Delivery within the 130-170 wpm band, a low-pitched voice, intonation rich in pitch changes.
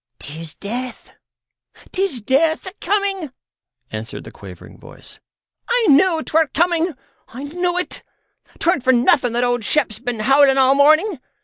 No: average, 140 wpm; very high, 285 Hz; wide, 6.1 semitones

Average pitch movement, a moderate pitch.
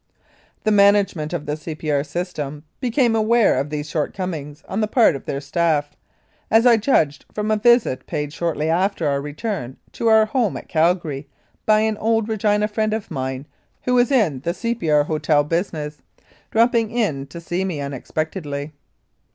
No: wide, 6.6 semitones; medium, 170 Hz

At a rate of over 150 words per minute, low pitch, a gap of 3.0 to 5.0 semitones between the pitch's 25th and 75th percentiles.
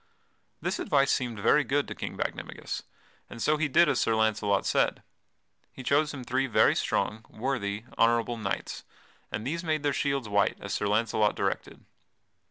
Yes: average, 170 wpm; low, 120 Hz; average, 4.7 semitones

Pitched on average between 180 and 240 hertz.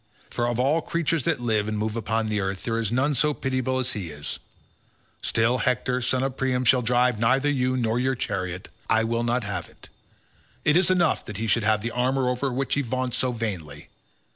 No: low, 120 Hz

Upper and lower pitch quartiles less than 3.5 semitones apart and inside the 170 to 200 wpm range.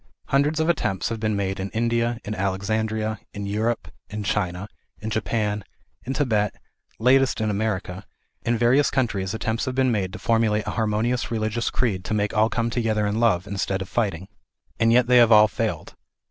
Yes: narrow, 2.4 semitones; average, 180 wpm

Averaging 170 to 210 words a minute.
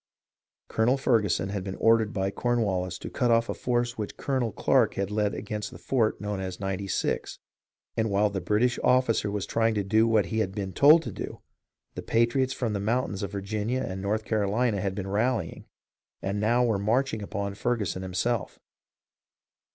Yes: average, 190 wpm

